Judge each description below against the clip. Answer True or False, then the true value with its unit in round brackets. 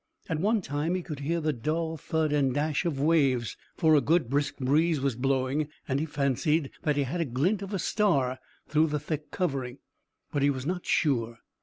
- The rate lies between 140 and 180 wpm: False (205 wpm)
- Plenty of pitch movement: False (3.1 semitones)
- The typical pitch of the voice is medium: True (150 Hz)